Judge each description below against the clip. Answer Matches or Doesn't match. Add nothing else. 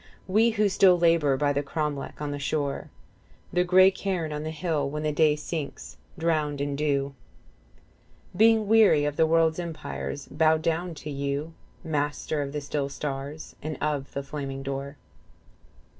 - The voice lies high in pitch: Doesn't match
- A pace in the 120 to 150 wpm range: Doesn't match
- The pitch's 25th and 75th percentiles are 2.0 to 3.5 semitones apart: Matches